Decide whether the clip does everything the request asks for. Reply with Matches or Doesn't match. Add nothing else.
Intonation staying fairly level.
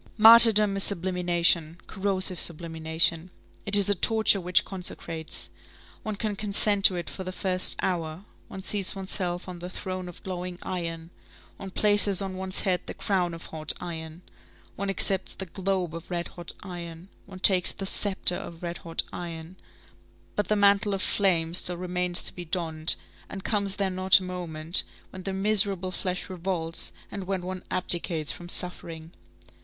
Matches